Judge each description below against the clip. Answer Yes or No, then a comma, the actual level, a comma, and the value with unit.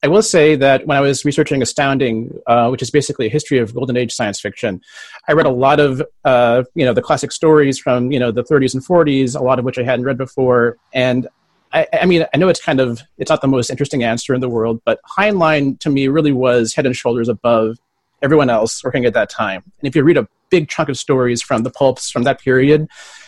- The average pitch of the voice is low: Yes, low, 130 Hz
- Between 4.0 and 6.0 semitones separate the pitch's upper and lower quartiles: No, average, 2.9 semitones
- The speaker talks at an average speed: No, fast, 245 wpm